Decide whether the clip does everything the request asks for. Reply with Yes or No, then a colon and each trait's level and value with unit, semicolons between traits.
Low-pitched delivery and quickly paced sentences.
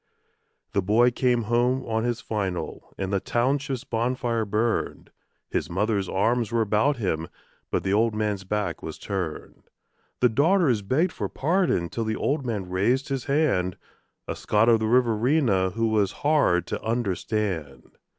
No: low, 115 Hz; average, 155 wpm